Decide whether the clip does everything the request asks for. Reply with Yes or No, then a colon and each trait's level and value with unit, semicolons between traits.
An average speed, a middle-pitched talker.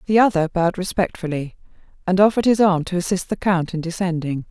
Yes: average, 185 wpm; medium, 180 Hz